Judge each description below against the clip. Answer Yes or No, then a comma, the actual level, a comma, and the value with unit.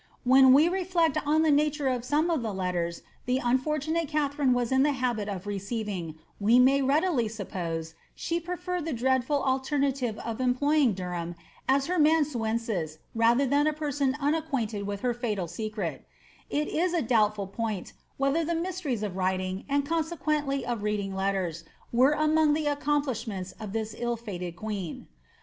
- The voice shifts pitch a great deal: Yes, wide, 6.2 semitones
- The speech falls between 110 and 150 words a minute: No, average, 170 wpm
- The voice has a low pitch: No, very high, 255 Hz